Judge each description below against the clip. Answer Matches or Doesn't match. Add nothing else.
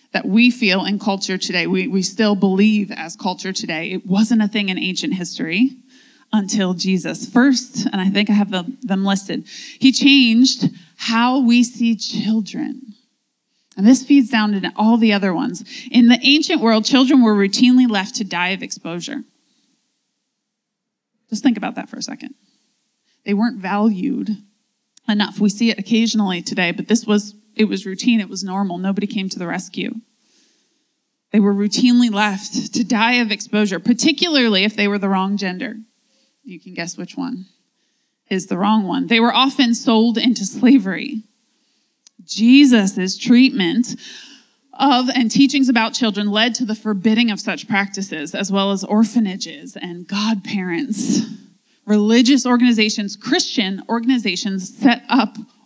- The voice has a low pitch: Doesn't match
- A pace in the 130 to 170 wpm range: Matches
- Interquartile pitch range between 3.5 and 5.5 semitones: Matches